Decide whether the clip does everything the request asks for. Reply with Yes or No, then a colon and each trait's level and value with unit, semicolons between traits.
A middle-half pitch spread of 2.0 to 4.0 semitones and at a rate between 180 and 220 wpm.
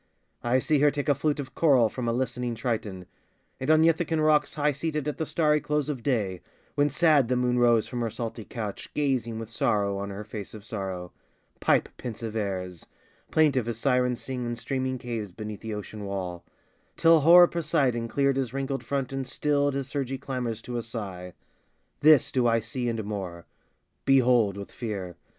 No: average, 4.6 semitones; average, 185 wpm